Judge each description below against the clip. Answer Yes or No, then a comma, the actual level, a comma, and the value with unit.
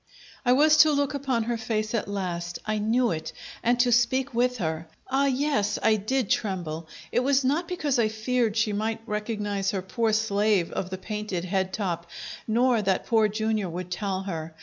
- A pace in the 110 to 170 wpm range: No, average, 190 wpm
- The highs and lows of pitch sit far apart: No, average, 4.4 semitones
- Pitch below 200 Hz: No, high, 215 Hz